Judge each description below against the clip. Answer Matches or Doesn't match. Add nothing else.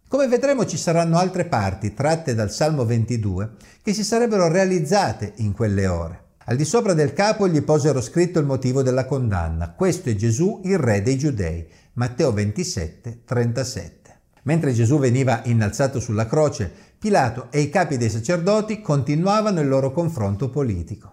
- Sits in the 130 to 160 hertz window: Matches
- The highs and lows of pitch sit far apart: Matches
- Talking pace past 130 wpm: Matches